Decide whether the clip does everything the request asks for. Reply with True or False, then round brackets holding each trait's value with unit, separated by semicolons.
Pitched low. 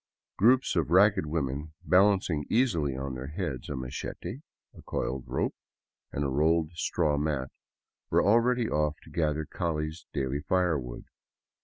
True (75 Hz)